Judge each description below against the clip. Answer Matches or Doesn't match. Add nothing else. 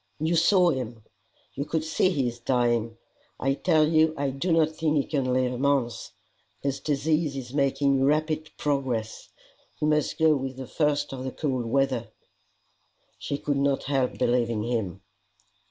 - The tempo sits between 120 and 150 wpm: Doesn't match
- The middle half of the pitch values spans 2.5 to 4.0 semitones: Matches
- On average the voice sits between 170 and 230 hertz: Doesn't match